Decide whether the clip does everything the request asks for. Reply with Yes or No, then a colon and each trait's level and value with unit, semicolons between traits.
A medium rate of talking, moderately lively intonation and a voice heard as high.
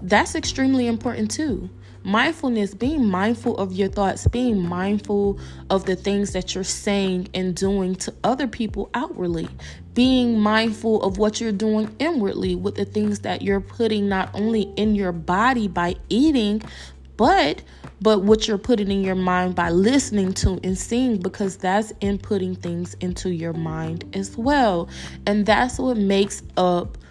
Yes: average, 155 wpm; average, 3.3 semitones; high, 200 Hz